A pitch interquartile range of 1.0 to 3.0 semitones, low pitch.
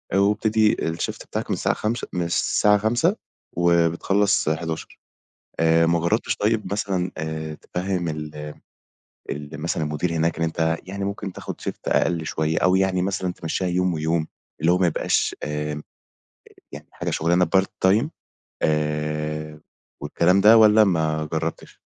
No: average, 3.7 semitones; very low, 85 Hz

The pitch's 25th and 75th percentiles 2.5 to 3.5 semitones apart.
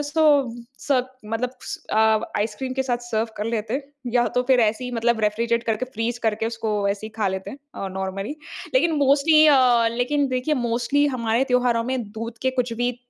Yes: average, 2.8 semitones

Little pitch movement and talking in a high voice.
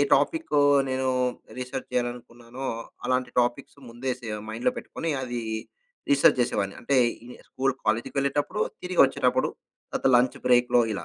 No: narrow, 2.0 semitones; low, 125 Hz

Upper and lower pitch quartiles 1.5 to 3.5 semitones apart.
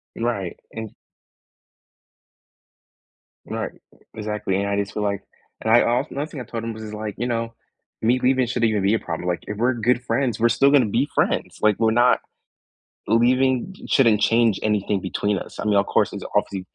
Yes: average, 2.7 semitones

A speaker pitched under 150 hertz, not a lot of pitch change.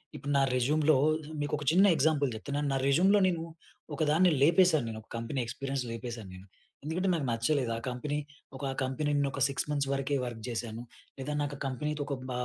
No: medium, 140 Hz; average, 3.5 semitones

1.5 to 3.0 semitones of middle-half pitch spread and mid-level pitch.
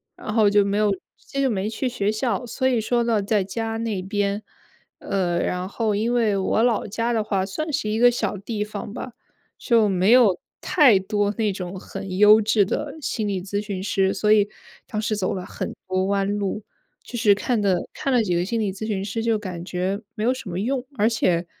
No: average, 2.7 semitones; high, 210 Hz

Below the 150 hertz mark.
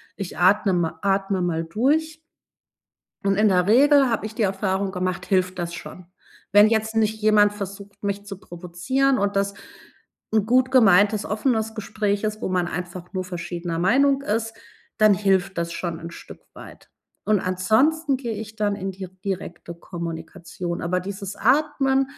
No: high, 200 Hz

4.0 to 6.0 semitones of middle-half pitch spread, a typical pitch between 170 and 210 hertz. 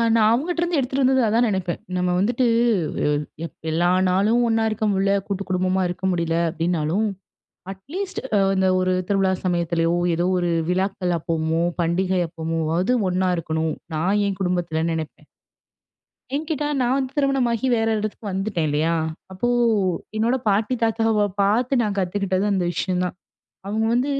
Yes: average, 4.4 semitones; high, 190 Hz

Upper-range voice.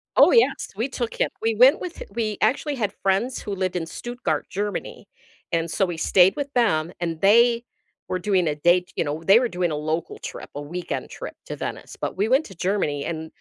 Yes: high, 195 Hz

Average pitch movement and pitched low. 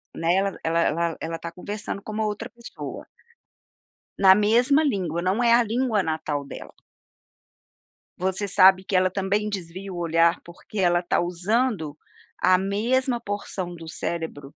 No: average, 3.8 semitones; high, 190 Hz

